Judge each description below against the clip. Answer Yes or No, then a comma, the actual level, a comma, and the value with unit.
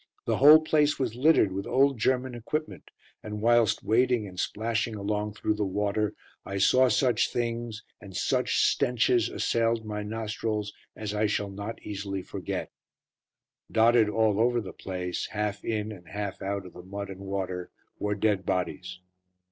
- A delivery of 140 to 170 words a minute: Yes, average, 160 wpm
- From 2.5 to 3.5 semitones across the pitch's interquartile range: Yes, average, 2.9 semitones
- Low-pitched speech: Yes, low, 105 Hz